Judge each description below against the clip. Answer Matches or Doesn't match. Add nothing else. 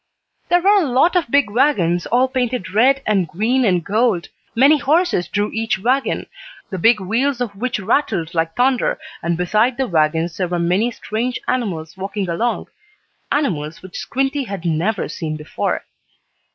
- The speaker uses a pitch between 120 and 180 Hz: Doesn't match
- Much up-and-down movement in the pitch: Matches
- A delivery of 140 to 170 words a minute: Matches